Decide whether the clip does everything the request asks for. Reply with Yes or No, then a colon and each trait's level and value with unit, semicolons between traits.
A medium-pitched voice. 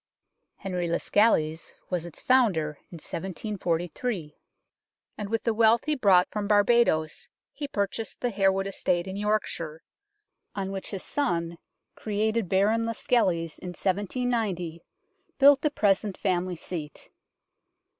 No: high, 195 Hz